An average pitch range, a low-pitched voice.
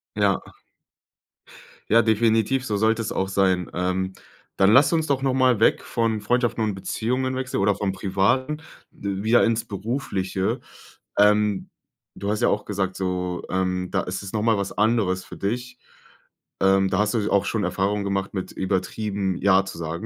Yes: average, 3.2 semitones; low, 100 Hz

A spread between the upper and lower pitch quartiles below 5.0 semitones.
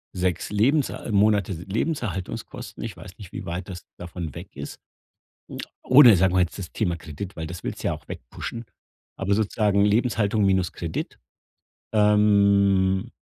Yes: average, 2.9 semitones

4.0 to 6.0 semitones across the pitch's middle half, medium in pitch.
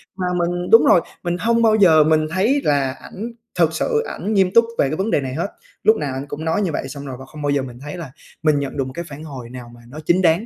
Yes: average, 5.1 semitones; medium, 160 Hz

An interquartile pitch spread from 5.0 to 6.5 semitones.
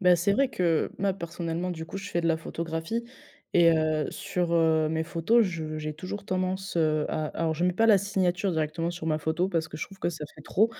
No: average, 2.7 semitones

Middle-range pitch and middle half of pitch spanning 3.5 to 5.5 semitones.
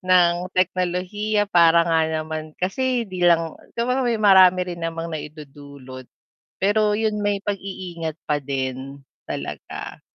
Yes: medium, 175 Hz; average, 4.3 semitones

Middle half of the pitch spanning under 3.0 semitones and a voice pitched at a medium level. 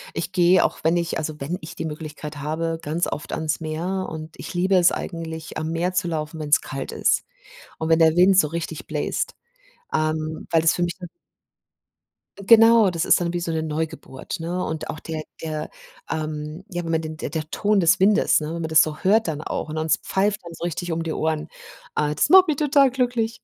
Yes: narrow, 2.5 semitones; medium, 165 Hz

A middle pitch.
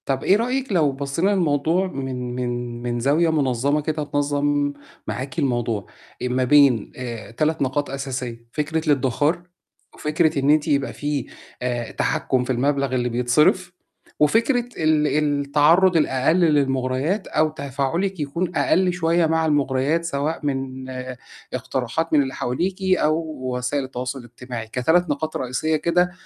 Yes: medium, 145 Hz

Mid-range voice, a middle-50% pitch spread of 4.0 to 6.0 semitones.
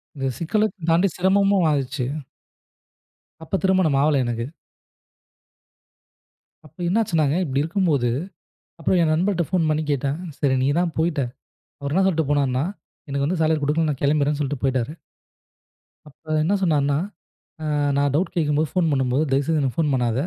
No: medium, 150 Hz; average, 3.2 semitones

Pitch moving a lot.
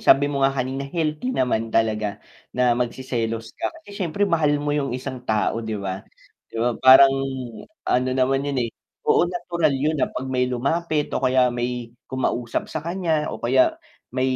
No: average, 3.7 semitones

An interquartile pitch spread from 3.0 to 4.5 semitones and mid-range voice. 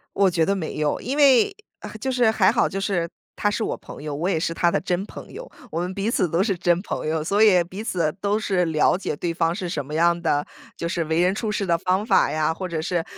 Yes: average, 3.4 semitones; medium, 180 Hz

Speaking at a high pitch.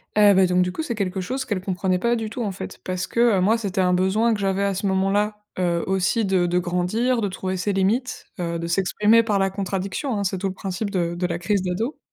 Yes: high, 195 Hz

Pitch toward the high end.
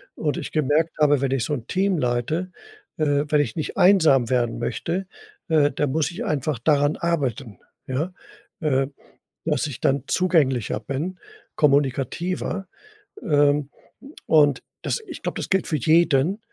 No: medium, 145 Hz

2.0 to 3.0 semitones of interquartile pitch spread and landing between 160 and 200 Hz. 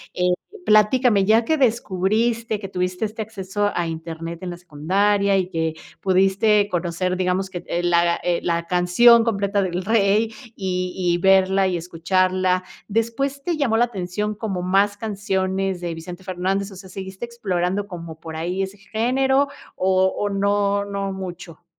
Yes: average, 2.7 semitones; high, 190 Hz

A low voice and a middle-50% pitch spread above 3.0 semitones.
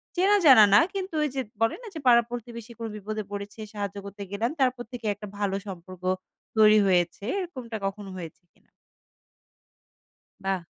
No: high, 215 Hz; average, 3.5 semitones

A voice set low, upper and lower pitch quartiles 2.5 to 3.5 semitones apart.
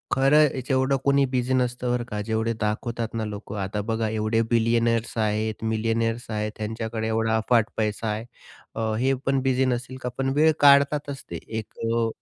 Yes: low, 115 Hz; average, 2.8 semitones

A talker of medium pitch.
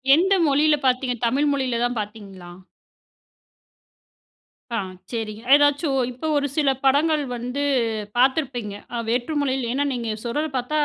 No: very high, 260 Hz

